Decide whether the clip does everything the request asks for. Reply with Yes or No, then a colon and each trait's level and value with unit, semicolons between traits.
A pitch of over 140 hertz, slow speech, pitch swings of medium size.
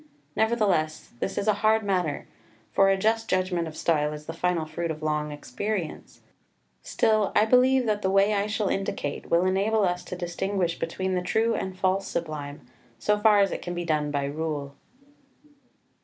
No: medium, 185 Hz; average, 180 wpm; average, 4.7 semitones